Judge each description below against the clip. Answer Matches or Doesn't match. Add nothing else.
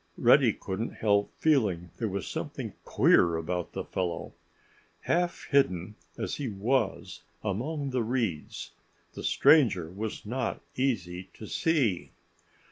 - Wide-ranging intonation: Matches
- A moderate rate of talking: Doesn't match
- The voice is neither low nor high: Doesn't match